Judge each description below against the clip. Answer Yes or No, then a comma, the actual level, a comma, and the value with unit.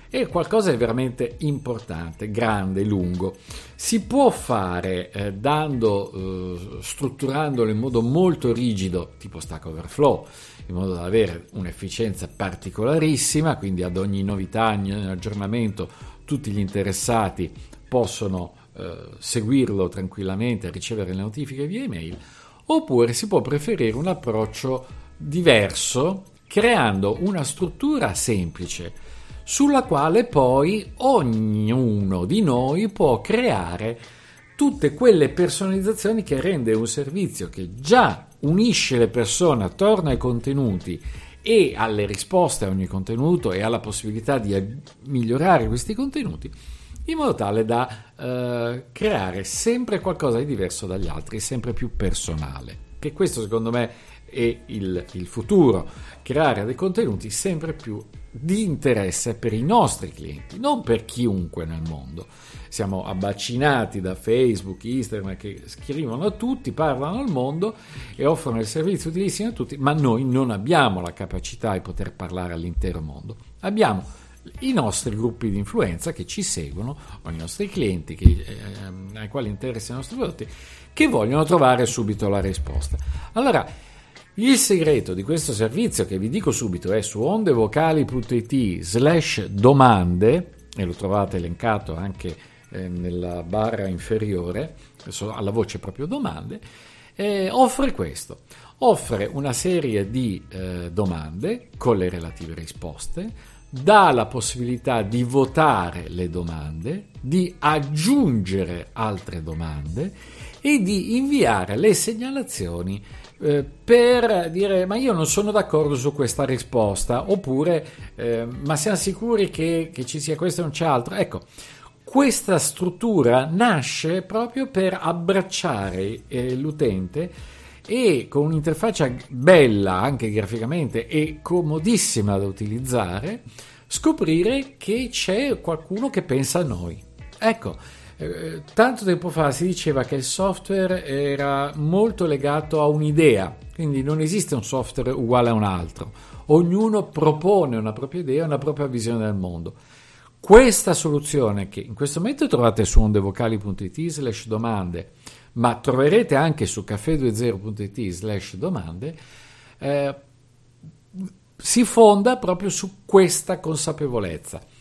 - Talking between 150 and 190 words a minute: No, average, 130 wpm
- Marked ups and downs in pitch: Yes, wide, 8.3 semitones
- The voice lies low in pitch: Yes, low, 125 Hz